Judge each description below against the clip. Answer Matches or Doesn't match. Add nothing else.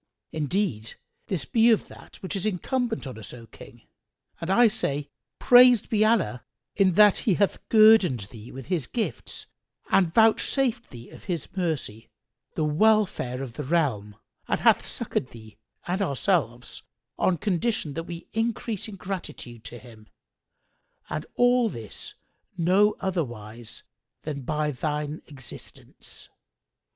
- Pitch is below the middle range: Doesn't match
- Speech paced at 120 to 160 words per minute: Matches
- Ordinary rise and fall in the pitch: Doesn't match